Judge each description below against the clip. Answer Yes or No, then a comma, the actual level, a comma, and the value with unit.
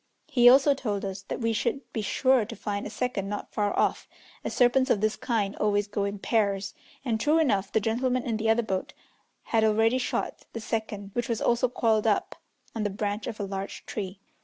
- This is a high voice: Yes, high, 220 Hz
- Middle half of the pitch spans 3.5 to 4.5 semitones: No, average, 3.0 semitones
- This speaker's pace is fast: Yes, fast, 210 wpm